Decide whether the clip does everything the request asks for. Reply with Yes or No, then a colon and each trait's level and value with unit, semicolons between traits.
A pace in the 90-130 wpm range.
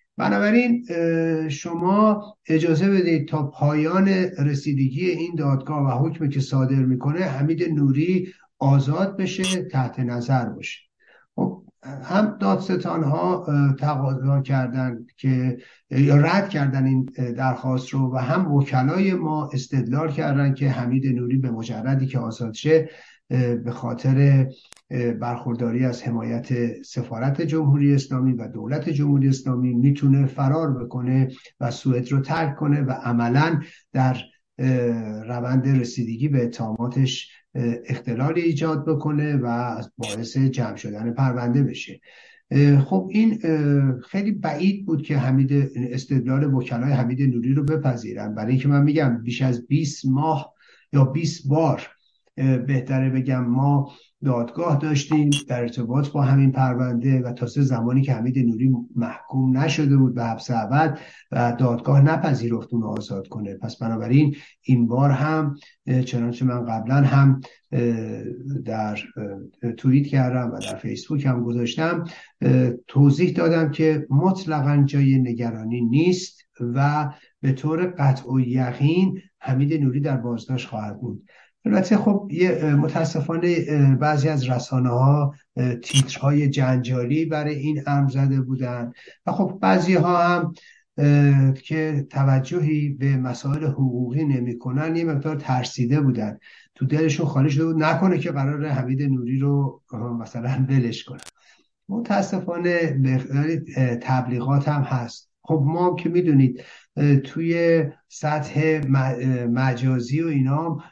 Yes: average, 125 wpm